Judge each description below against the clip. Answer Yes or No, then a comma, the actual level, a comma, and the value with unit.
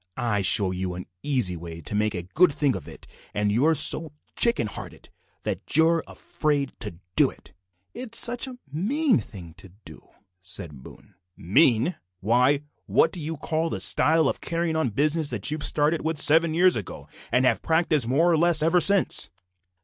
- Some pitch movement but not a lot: No, wide, 7.7 semitones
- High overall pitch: No, medium, 145 Hz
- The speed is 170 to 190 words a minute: Yes, average, 180 wpm